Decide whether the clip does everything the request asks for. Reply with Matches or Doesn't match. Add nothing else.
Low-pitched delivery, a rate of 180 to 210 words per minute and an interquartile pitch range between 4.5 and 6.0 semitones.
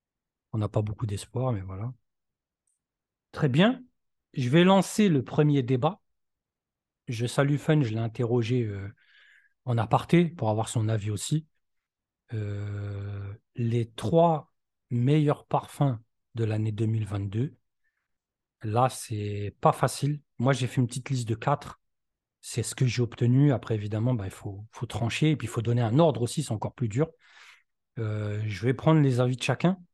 Doesn't match